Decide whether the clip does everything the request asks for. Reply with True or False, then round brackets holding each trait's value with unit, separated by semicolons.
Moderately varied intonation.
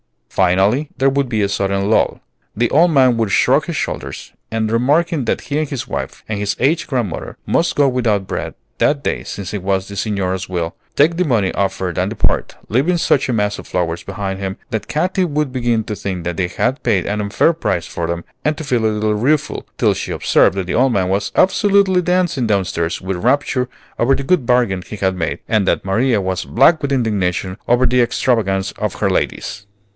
False (5.9 semitones)